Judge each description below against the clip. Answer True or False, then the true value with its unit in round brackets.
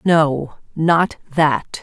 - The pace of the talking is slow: True (100 wpm)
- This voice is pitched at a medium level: True (155 Hz)